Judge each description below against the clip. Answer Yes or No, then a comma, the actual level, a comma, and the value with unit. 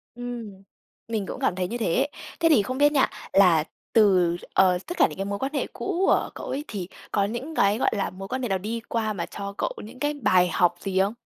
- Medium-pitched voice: No, high, 210 Hz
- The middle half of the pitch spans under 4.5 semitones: No, average, 5.1 semitones